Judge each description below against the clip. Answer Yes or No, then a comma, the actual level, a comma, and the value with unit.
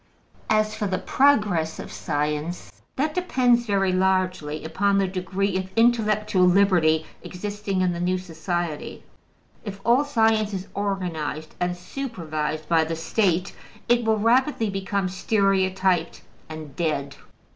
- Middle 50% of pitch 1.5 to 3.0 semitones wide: No, average, 3.8 semitones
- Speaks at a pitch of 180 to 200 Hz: Yes, high, 190 Hz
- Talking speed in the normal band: No, slow, 130 wpm